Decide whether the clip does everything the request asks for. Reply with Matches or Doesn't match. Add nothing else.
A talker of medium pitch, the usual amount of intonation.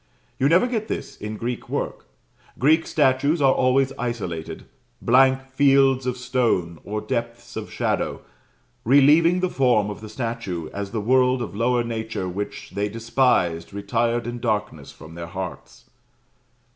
Doesn't match